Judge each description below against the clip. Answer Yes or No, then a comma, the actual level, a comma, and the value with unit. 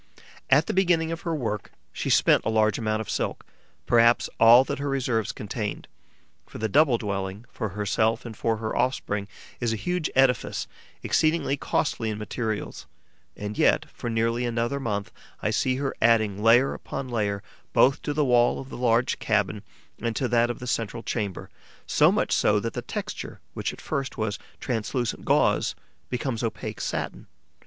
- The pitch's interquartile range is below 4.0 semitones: Yes, average, 3.3 semitones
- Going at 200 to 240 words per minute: No, average, 175 wpm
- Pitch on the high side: No, low, 115 Hz